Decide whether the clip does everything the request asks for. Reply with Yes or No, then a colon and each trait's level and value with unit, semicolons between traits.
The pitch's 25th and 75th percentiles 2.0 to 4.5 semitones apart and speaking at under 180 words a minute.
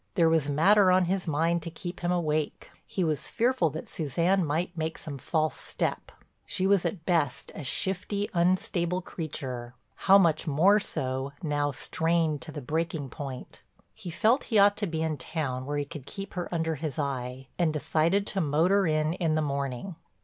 No: average, 3.7 semitones; average, 185 wpm